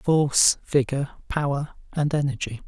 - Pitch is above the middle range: No, medium, 140 Hz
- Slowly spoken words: Yes, slow, 110 wpm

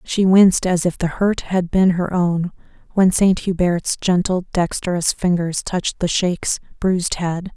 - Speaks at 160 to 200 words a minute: Yes, average, 165 wpm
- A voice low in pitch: No, medium, 180 Hz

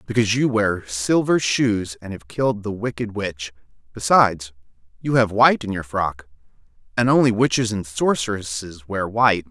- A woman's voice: No, male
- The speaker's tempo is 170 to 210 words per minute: No, average, 160 wpm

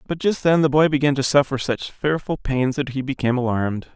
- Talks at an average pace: No, fast, 230 wpm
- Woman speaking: No, male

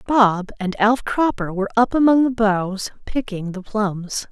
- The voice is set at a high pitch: Yes, high, 215 Hz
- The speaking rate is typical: Yes, average, 165 wpm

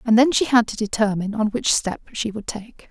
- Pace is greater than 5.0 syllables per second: Yes, 5.5 syllables/s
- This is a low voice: No, high, 220 Hz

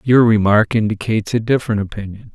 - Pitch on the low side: Yes, low, 110 Hz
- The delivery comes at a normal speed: Yes, average, 155 wpm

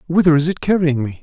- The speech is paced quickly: Yes, fast, 245 wpm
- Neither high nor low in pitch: Yes, medium, 160 Hz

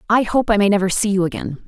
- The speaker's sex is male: No, female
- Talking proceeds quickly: Yes, fast, 285 wpm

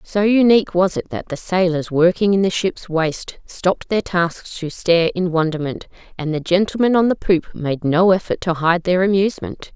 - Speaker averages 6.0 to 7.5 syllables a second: No, 5.0 syllables/s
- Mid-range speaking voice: Yes, medium, 180 Hz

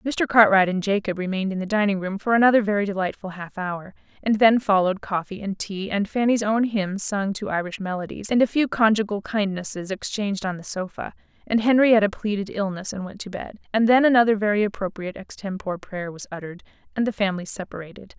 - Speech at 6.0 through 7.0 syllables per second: Yes, 6.1 syllables/s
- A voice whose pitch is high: Yes, high, 200 Hz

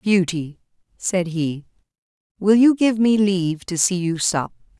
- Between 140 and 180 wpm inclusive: Yes, average, 150 wpm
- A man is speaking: No, female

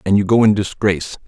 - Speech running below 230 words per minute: No, fast, 235 wpm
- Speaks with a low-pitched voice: Yes, low, 100 Hz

